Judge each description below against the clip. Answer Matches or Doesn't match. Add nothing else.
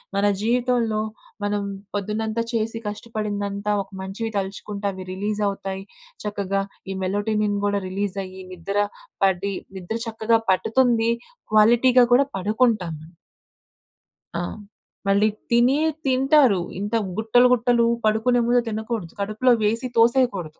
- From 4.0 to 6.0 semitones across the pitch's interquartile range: Doesn't match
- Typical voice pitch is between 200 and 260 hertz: Matches